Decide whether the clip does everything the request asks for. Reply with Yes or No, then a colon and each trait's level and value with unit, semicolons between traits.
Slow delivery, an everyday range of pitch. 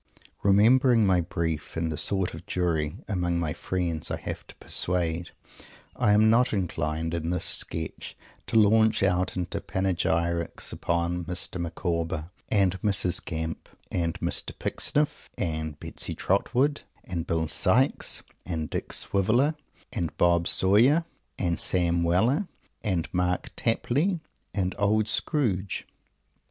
Yes: slow, 130 wpm; average, 3.7 semitones